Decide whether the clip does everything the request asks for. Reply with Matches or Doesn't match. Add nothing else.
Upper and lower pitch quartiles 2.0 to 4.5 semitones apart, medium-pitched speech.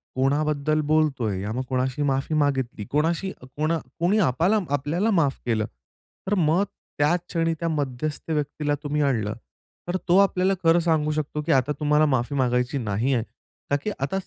Matches